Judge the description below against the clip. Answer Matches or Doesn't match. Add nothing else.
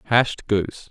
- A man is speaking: Matches